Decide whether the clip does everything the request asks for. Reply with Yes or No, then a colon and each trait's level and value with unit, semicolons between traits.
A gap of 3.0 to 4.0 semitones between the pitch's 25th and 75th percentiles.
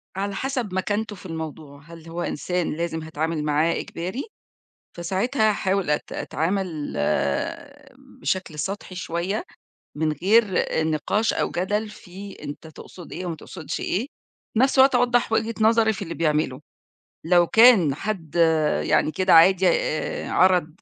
No: average, 4.5 semitones